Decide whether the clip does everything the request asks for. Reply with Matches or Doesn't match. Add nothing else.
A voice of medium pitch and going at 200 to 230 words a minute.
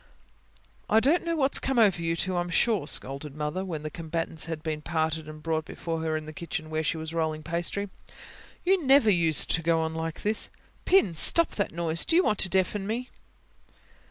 Matches